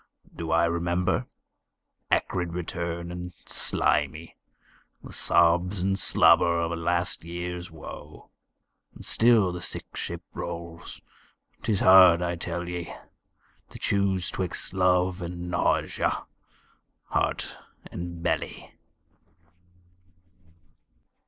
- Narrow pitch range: Yes, narrow, 1.1 semitones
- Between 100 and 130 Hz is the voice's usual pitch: No, very low, 85 Hz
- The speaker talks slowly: Yes, slow, 100 wpm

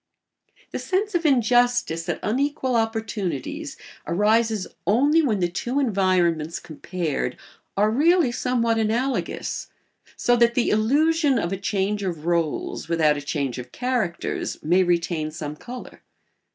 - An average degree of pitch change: No, wide, 6.8 semitones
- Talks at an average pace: No, slow, 130 wpm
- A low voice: No, high, 215 Hz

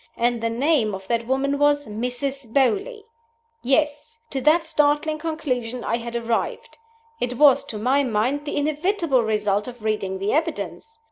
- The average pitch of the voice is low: No, very high, 265 Hz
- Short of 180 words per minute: Yes, average, 155 wpm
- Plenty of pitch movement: No, average, 4.5 semitones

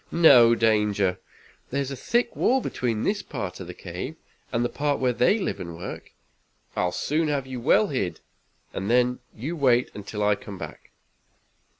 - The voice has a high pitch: No, low, 120 Hz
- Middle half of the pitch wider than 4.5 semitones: Yes, wide, 5.6 semitones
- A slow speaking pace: No, average, 180 wpm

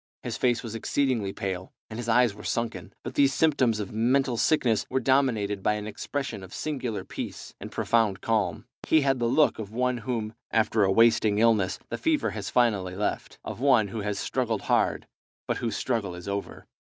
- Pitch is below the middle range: Yes, low, 115 Hz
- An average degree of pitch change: Yes, average, 3.5 semitones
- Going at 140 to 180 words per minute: No, average, 190 wpm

